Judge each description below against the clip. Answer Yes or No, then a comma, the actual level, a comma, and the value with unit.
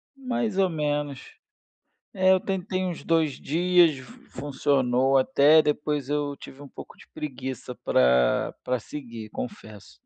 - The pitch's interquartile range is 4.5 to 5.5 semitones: Yes, average, 5.2 semitones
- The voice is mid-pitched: Yes, medium, 145 Hz